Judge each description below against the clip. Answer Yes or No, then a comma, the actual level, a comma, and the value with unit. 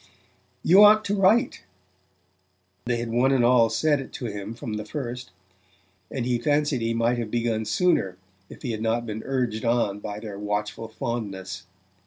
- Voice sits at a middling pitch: No, low, 115 Hz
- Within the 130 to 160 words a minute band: No, average, 175 wpm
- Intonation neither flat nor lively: Yes, average, 3.2 semitones